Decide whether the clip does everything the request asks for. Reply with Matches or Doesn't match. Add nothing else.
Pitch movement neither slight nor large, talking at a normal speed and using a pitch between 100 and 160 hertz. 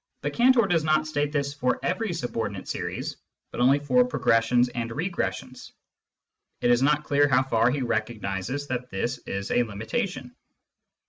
Matches